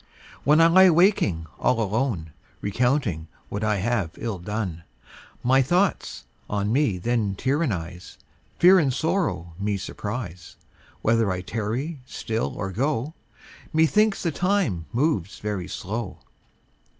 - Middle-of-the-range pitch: No, low, 115 Hz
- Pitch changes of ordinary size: No, wide, 7.5 semitones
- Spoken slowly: Yes, slow, 125 wpm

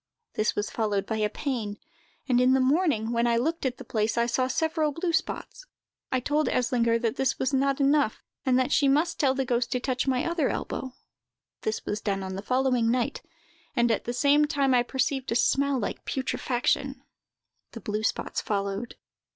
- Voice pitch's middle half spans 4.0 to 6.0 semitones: No, average, 3.1 semitones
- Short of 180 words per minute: No, average, 195 wpm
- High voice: Yes, very high, 255 Hz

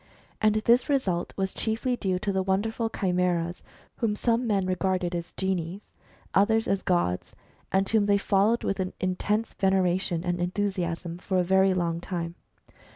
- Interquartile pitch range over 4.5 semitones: No, average, 2.8 semitones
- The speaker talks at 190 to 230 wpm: No, average, 155 wpm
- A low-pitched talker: No, high, 190 Hz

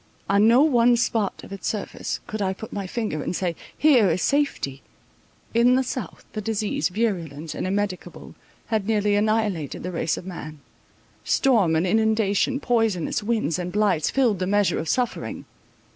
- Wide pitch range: No, average, 4.0 semitones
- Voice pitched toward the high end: Yes, high, 205 Hz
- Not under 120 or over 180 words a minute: Yes, average, 170 wpm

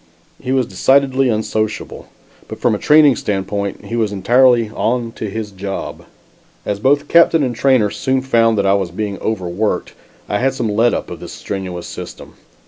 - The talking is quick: No, average, 175 wpm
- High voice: No, low, 110 Hz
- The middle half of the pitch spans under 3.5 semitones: No, average, 4.4 semitones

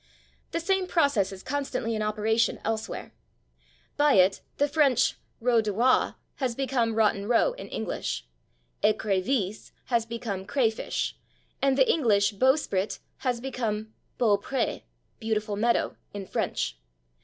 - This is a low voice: No, high, 230 Hz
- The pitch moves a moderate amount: Yes, average, 4.1 semitones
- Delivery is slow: Yes, slow, 130 wpm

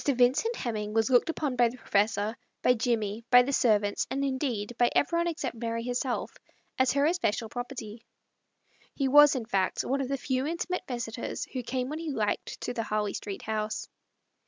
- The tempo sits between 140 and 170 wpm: No, average, 185 wpm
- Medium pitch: No, high, 245 Hz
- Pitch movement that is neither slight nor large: Yes, average, 3.8 semitones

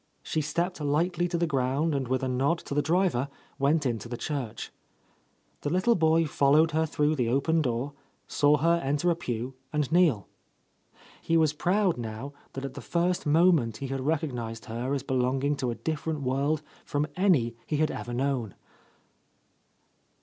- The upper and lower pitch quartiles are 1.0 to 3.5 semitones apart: No, average, 4.0 semitones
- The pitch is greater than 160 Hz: No, medium, 145 Hz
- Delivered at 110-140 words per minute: No, average, 175 wpm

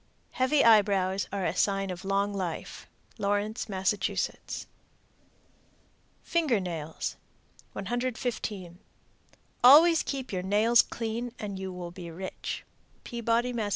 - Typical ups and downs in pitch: Yes, average, 4.0 semitones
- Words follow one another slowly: Yes, slow, 110 wpm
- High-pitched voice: Yes, high, 205 Hz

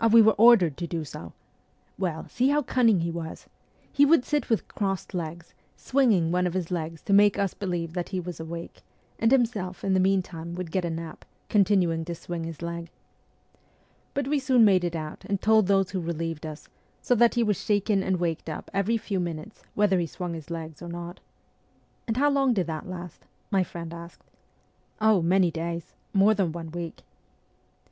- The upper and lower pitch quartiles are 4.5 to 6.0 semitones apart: No, average, 3.8 semitones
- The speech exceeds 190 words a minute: Yes, average, 200 wpm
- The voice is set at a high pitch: No, medium, 180 Hz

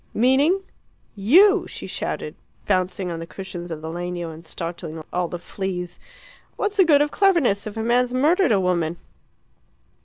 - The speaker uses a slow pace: No, average, 165 wpm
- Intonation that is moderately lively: No, wide, 7.9 semitones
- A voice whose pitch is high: Yes, high, 195 Hz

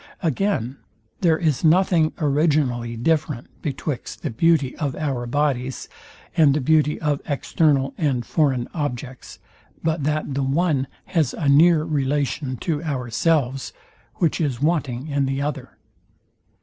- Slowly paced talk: Yes, slow, 130 wpm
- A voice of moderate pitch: Yes, medium, 145 Hz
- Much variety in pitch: No, average, 3.0 semitones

